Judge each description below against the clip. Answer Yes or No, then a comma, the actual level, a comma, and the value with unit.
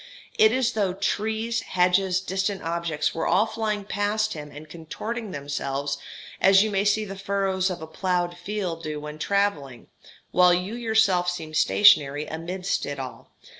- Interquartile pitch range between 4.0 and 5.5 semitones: Yes, average, 4.4 semitones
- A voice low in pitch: No, medium, 185 Hz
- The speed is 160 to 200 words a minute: Yes, average, 165 wpm